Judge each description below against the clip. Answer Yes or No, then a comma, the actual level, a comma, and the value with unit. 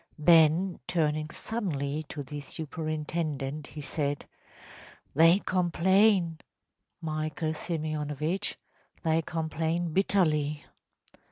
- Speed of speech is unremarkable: No, slow, 85 wpm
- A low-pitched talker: No, medium, 160 Hz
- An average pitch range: No, narrow, 2.3 semitones